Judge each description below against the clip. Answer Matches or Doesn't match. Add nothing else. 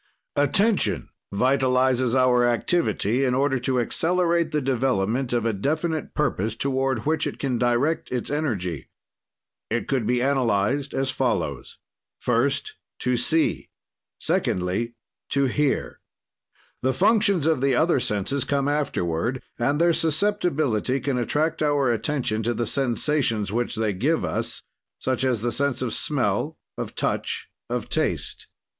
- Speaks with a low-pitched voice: Matches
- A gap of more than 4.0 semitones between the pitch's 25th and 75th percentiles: Doesn't match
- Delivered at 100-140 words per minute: Matches